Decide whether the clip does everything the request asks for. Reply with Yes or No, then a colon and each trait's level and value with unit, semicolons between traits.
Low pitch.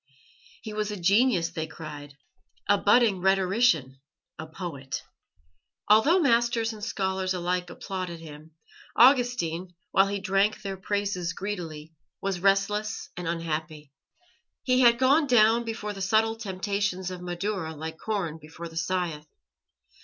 No: high, 190 Hz